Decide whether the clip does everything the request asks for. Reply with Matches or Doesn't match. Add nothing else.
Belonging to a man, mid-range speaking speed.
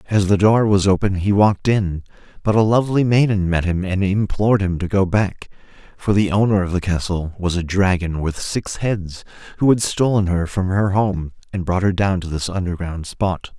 Doesn't match